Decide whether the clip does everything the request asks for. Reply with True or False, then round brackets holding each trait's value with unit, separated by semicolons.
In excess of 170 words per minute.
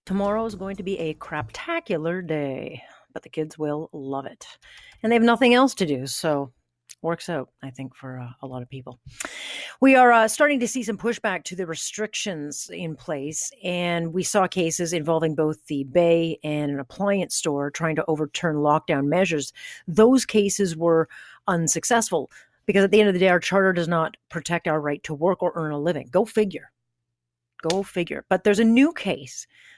True (190 wpm)